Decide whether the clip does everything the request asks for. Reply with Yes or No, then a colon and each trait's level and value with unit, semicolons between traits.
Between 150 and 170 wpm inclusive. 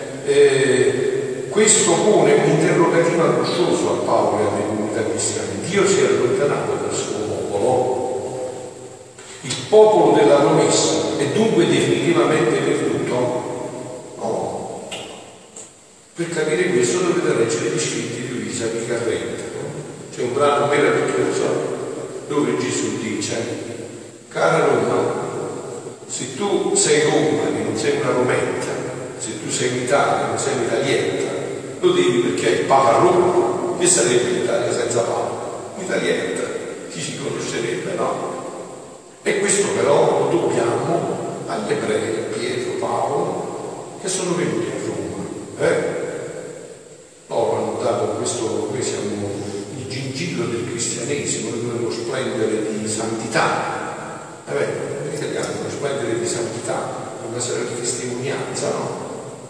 No: average, 130 wpm